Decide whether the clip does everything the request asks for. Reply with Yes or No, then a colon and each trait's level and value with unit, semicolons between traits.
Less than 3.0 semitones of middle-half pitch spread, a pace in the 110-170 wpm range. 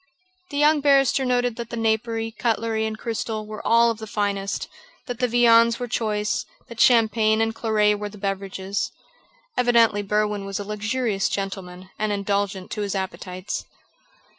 Yes: narrow, 2.4 semitones; average, 160 wpm